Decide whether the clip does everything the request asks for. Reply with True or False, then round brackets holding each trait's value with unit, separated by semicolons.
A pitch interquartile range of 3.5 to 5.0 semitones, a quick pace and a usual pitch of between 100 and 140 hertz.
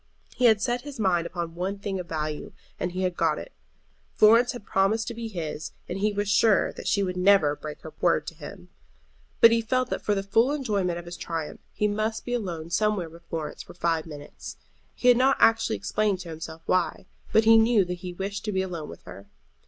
False (4.5 semitones; 225 wpm; 190 Hz)